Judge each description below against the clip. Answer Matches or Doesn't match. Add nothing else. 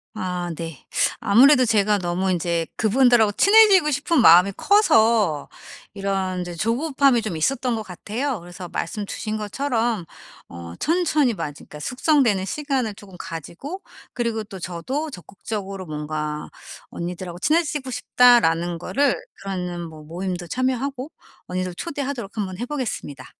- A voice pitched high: Matches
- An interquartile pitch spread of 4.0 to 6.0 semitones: Doesn't match